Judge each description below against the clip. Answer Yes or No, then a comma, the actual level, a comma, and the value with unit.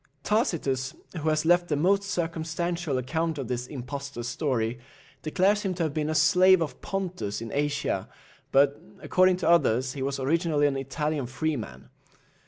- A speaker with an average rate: Yes, average, 160 wpm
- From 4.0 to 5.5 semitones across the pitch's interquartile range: Yes, average, 4.3 semitones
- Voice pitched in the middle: Yes, medium, 155 Hz